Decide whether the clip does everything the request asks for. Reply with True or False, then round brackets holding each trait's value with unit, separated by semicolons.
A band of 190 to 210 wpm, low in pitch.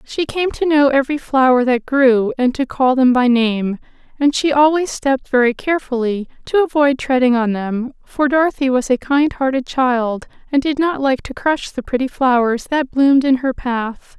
False (195 wpm; 270 Hz)